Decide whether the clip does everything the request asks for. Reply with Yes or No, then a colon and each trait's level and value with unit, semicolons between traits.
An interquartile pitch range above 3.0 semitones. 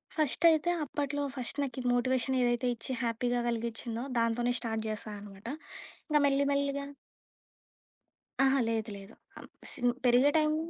Yes: average, 3.4 semitones